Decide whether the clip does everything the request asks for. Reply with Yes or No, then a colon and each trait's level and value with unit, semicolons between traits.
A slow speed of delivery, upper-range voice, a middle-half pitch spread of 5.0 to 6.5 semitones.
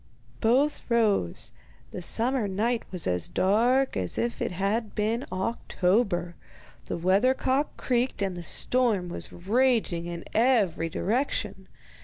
Yes: slow, 130 wpm; high, 215 Hz; wide, 5.4 semitones